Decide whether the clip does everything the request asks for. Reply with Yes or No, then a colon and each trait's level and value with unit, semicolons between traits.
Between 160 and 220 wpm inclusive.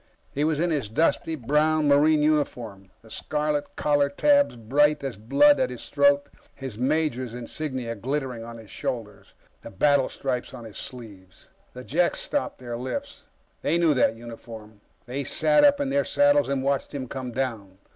Yes: average, 170 wpm